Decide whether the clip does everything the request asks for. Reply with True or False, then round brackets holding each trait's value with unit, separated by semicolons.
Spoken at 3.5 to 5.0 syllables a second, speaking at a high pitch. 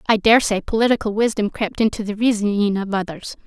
False (6.2 syllables/s; 210 Hz)